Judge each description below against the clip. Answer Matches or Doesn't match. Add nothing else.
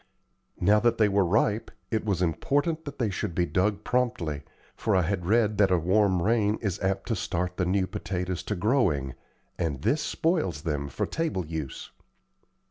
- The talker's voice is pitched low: Matches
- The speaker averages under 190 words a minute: Matches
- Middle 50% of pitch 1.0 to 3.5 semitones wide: Doesn't match